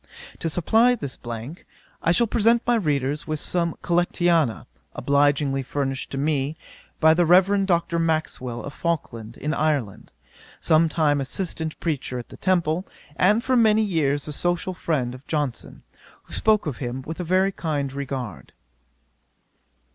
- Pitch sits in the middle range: Yes, medium, 155 Hz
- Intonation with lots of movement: No, average, 4.2 semitones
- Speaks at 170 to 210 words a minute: No, average, 150 wpm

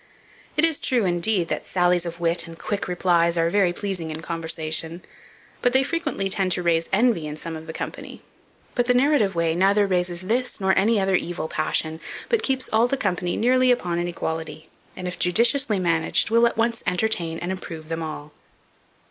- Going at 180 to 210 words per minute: Yes, average, 190 wpm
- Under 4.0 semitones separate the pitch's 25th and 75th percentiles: No, average, 5.0 semitones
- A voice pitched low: No, medium, 180 Hz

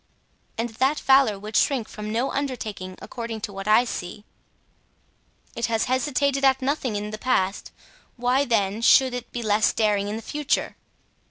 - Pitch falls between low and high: No, high, 230 Hz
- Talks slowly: No, average, 165 wpm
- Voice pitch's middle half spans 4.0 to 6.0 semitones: No, average, 3.6 semitones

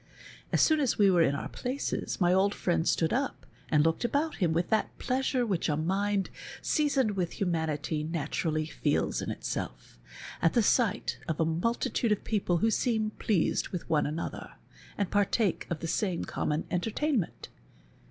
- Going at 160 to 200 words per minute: Yes, average, 170 wpm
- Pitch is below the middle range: No, high, 190 Hz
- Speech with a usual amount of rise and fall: No, wide, 5.7 semitones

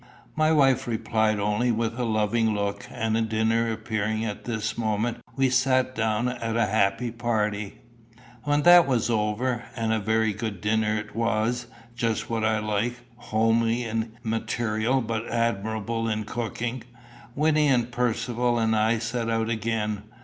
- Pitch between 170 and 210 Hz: No, low, 115 Hz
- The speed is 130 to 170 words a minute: Yes, average, 150 wpm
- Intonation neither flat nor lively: No, narrow, 1.7 semitones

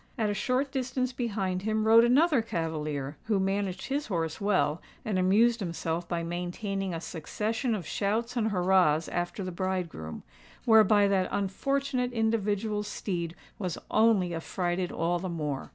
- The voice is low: No, high, 195 Hz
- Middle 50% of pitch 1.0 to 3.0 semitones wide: No, average, 4.3 semitones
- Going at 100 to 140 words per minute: No, average, 150 wpm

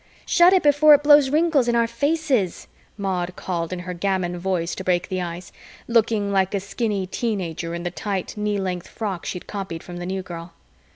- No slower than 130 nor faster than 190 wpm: No, fast, 205 wpm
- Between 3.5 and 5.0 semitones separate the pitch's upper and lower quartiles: Yes, average, 4.7 semitones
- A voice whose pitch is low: No, high, 190 Hz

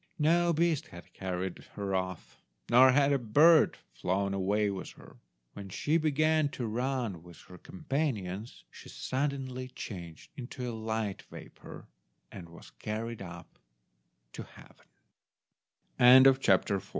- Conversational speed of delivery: No, slow, 125 wpm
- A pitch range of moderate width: No, wide, 6.4 semitones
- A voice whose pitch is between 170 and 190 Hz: No, low, 115 Hz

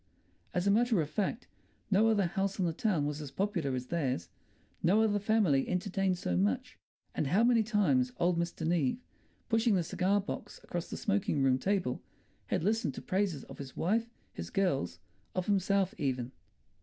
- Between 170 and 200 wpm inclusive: Yes, average, 180 wpm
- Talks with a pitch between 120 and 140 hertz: No, medium, 180 Hz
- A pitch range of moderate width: No, wide, 6.2 semitones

